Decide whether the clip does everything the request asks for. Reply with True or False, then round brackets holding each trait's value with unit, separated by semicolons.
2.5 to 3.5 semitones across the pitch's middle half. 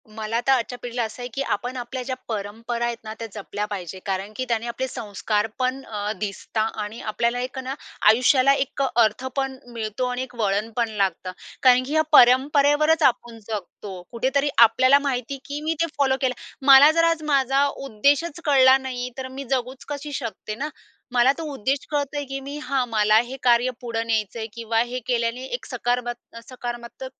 True (3.1 semitones)